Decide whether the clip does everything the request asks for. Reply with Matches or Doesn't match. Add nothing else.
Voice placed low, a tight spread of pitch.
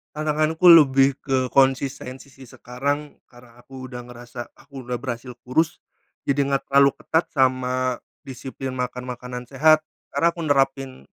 Matches